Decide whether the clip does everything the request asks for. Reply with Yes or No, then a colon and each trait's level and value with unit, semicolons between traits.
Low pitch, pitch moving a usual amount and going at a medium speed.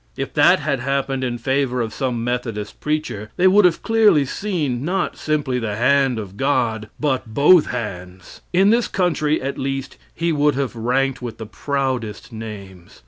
Yes: low, 130 Hz; average, 4.7 semitones; average, 170 wpm